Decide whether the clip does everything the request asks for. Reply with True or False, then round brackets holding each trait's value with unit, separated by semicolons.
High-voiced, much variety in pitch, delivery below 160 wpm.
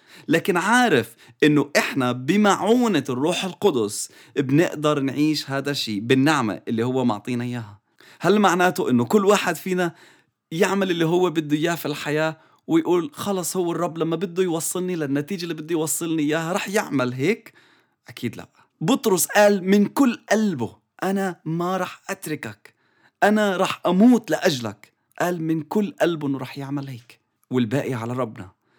False (160 Hz; 5.9 semitones; 145 wpm)